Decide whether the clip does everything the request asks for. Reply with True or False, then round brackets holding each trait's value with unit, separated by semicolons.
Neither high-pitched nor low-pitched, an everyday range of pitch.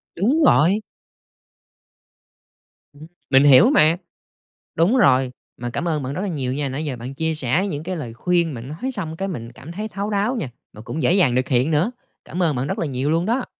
False (155 Hz; 6.0 semitones)